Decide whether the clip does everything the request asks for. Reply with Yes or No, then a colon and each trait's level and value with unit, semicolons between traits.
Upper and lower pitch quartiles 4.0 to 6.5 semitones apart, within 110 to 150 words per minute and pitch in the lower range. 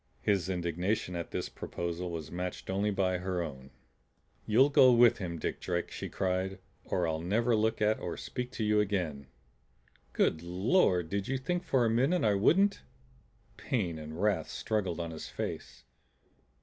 No: average, 4.5 semitones; average, 165 wpm; very low, 95 Hz